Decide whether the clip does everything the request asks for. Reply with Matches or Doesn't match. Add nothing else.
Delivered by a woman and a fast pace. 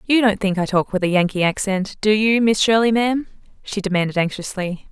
Matches